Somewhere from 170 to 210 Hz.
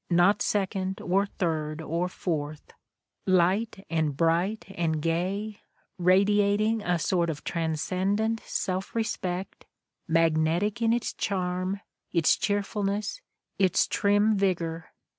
Yes: medium, 185 Hz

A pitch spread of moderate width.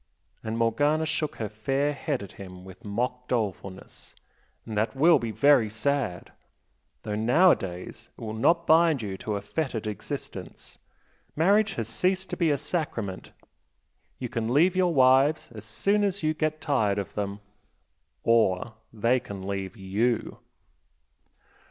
No: wide, 6.8 semitones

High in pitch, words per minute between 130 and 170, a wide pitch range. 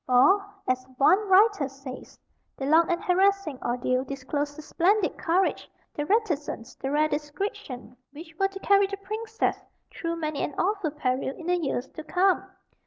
Yes: very high, 320 Hz; average, 165 wpm; wide, 6.0 semitones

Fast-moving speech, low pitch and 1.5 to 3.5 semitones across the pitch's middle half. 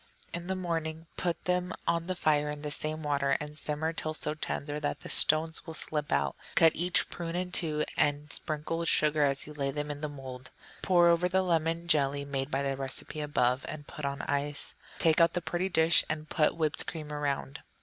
No: fast, 215 wpm; medium, 155 Hz; narrow, 2.4 semitones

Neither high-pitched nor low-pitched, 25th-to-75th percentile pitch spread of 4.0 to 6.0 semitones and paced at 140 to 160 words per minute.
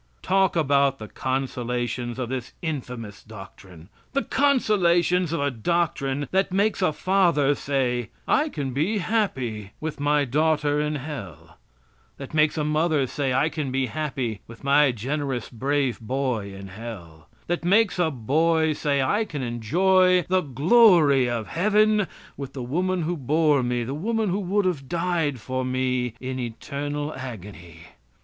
Yes: medium, 145 Hz; wide, 5.5 semitones; average, 155 wpm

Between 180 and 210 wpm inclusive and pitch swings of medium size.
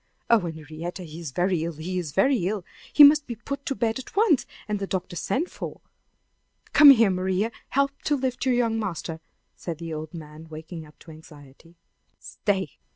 No: average, 195 wpm; wide, 7.0 semitones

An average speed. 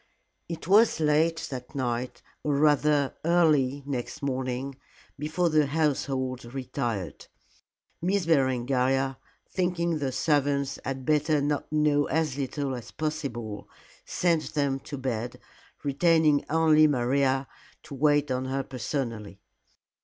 No: slow, 115 wpm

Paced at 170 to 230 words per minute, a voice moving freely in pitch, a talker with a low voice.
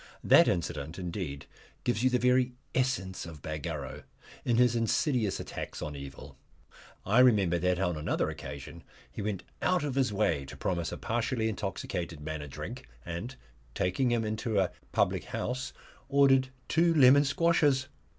No: average, 155 wpm; wide, 7.0 semitones; low, 110 Hz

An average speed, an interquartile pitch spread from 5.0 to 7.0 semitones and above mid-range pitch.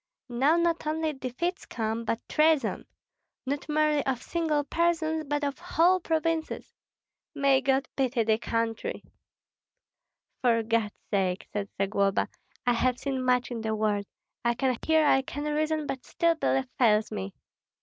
Yes: average, 150 wpm; average, 5.3 semitones; very high, 270 Hz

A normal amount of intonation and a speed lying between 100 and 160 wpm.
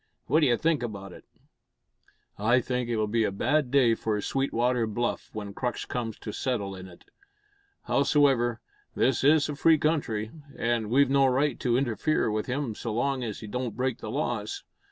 No: average, 3.9 semitones; average, 175 wpm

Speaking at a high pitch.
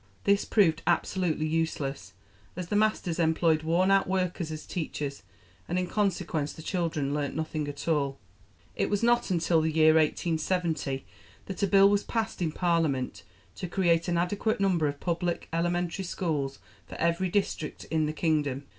No: medium, 165 Hz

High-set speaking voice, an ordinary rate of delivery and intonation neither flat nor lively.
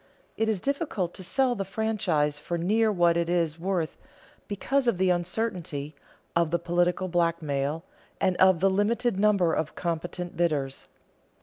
No: medium, 175 Hz; average, 150 wpm; average, 3.5 semitones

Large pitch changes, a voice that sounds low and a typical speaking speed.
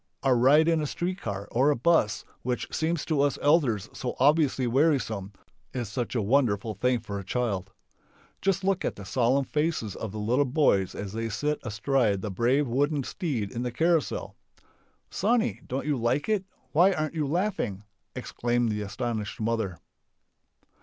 Yes: wide, 5.7 semitones; low, 125 Hz; average, 170 wpm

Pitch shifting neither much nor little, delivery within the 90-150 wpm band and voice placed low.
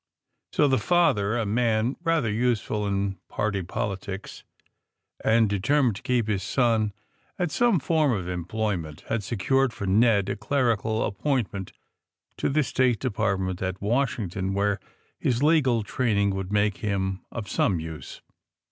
Yes: average, 4.3 semitones; average, 140 wpm; low, 110 Hz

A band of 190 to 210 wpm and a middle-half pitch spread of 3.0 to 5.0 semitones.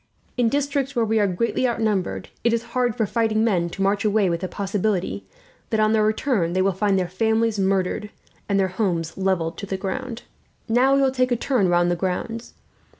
Yes: average, 195 wpm; average, 3.7 semitones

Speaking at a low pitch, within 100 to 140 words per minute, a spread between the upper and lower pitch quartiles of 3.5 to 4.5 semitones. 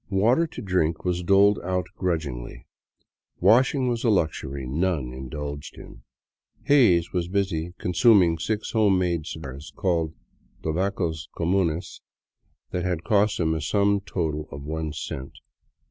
Yes: very low, 85 Hz; slow, 135 wpm; average, 3.9 semitones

